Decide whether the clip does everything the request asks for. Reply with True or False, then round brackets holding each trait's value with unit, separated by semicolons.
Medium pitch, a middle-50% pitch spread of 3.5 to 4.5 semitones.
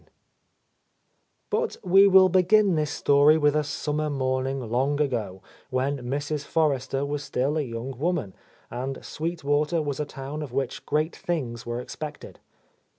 False (145 Hz; 2.8 semitones)